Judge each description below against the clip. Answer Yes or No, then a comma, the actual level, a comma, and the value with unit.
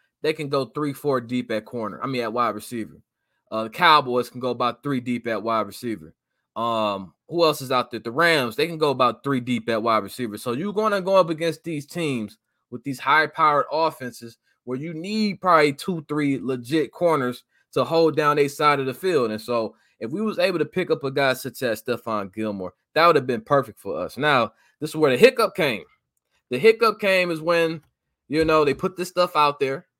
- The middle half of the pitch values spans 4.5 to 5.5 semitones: Yes, average, 5.2 semitones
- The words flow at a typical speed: No, fast, 220 wpm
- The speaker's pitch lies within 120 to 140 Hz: Yes, low, 135 Hz